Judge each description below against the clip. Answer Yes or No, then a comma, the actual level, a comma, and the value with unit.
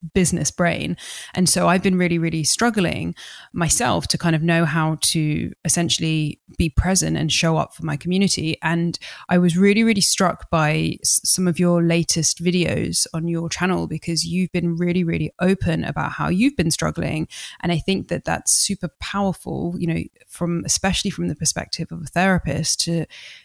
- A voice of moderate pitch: Yes, medium, 170 Hz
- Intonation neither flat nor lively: No, narrow, 2.0 semitones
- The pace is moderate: Yes, average, 175 wpm